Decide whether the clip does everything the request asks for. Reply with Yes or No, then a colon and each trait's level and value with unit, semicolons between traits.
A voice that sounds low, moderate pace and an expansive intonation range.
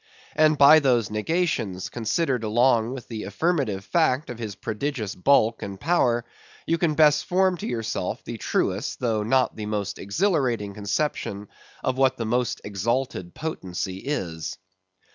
Yes: low, 120 Hz; average, 145 wpm; wide, 6.0 semitones